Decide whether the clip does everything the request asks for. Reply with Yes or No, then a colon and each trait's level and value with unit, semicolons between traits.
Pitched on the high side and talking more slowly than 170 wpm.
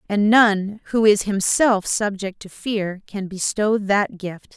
Yes: high, 205 Hz; average, 160 wpm